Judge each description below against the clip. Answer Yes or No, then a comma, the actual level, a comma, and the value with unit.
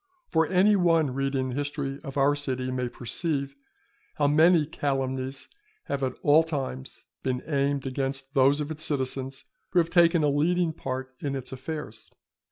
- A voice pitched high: No, medium, 140 Hz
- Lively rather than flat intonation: No, average, 3.0 semitones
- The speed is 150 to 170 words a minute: Yes, average, 165 wpm